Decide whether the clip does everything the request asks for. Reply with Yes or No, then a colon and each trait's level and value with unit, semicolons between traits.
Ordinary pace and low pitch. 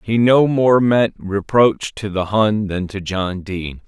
Yes: average, 185 wpm; low, 105 Hz